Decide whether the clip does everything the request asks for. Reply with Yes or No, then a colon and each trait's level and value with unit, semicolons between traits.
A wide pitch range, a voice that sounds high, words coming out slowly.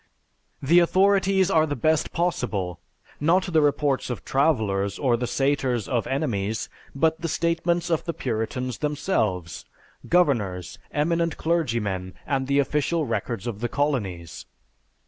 No: wide, 6.8 semitones; medium, 140 Hz; slow, 130 wpm